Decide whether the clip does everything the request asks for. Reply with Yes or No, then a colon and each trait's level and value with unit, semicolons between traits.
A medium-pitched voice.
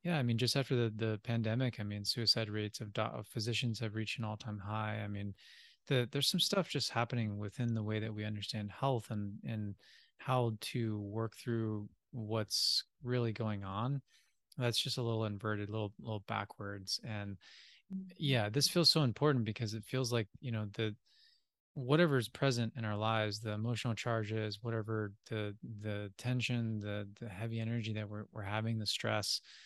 No: low, 110 Hz